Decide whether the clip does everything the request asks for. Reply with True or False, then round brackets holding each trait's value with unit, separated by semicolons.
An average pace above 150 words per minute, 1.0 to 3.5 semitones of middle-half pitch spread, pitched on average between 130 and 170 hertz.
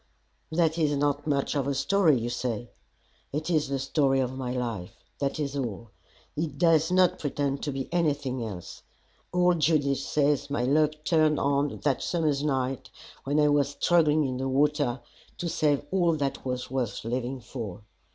True (170 wpm; 2.8 semitones; 140 Hz)